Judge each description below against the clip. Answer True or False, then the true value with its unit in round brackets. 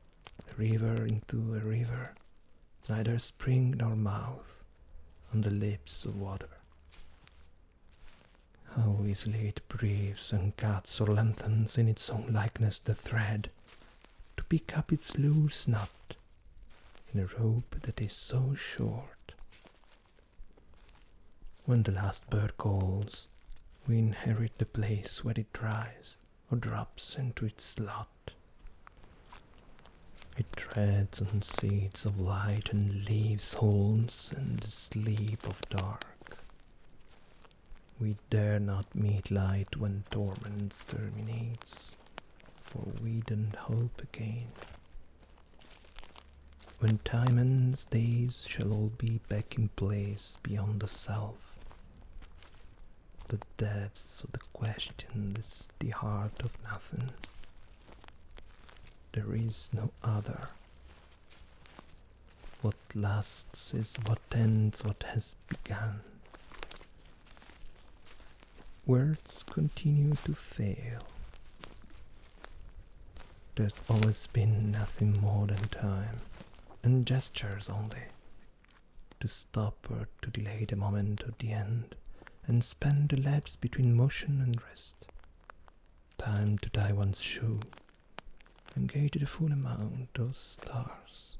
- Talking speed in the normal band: False (105 wpm)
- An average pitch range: True (3.4 semitones)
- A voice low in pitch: True (105 Hz)